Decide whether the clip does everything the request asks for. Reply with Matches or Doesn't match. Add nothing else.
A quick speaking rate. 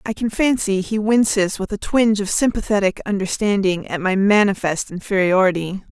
Doesn't match